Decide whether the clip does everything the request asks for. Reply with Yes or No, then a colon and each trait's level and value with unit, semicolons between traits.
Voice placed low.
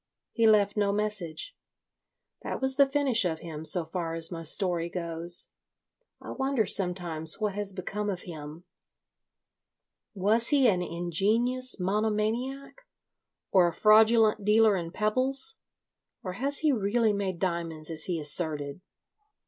No: high, 200 Hz